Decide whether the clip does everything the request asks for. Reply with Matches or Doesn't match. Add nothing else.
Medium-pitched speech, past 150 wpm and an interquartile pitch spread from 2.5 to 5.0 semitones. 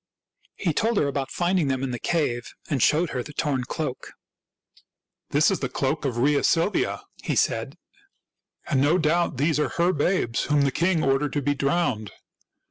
Matches